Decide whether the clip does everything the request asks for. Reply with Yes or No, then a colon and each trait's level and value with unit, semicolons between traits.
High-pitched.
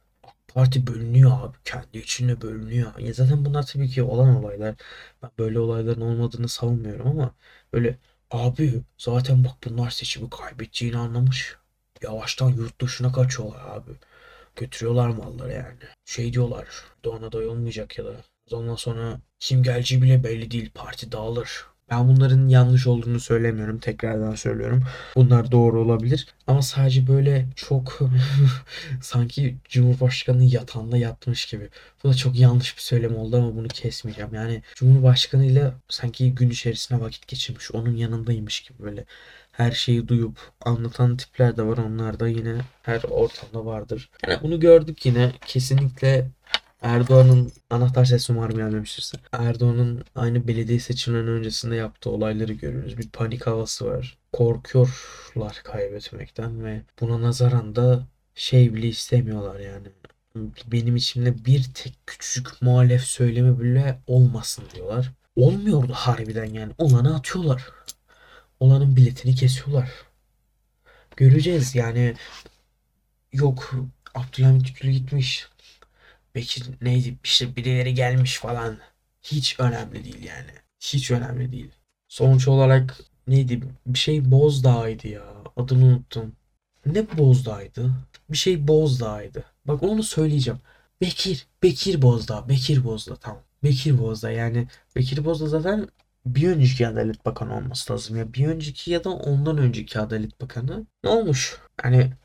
No: low, 125 Hz